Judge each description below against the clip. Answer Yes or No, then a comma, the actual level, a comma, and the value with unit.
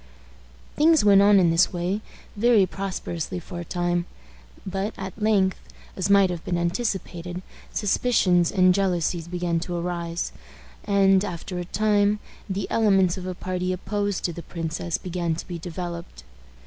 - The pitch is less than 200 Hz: Yes, medium, 185 Hz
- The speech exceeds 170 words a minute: No, average, 150 wpm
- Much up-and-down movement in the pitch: No, narrow, 2.4 semitones